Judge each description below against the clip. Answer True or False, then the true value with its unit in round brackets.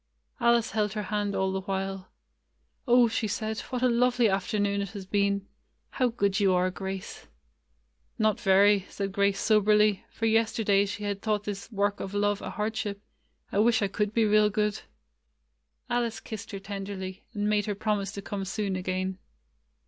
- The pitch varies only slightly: True (1.7 semitones)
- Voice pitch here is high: True (205 Hz)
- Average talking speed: True (180 wpm)